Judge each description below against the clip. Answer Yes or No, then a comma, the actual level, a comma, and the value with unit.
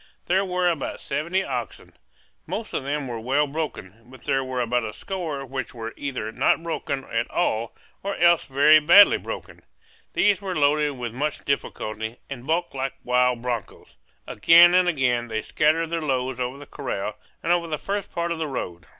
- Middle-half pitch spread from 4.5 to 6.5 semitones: Yes, average, 5.3 semitones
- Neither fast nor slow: Yes, average, 185 wpm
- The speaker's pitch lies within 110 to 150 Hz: Yes, medium, 140 Hz